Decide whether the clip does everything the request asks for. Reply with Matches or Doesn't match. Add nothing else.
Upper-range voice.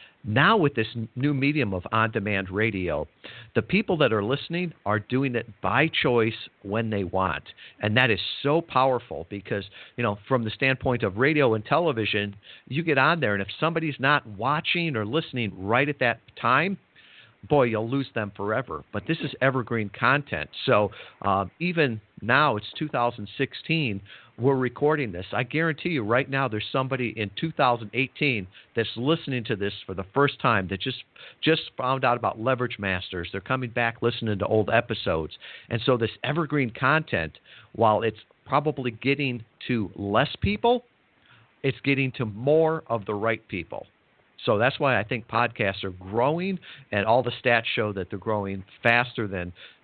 Doesn't match